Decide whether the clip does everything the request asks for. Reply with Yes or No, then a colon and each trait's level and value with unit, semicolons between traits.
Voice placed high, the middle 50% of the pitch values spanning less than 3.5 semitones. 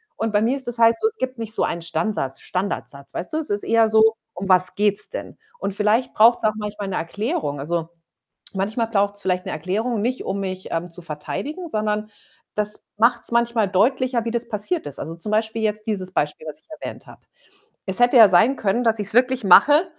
No: high, 210 Hz; average, 4.0 semitones